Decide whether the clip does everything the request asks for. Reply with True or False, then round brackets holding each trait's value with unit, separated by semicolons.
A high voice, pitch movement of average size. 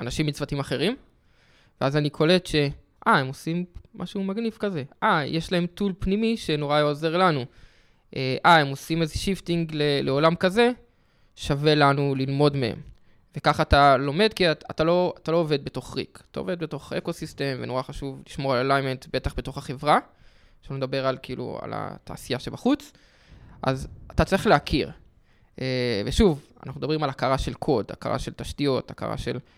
False (150 Hz; 4.5 semitones)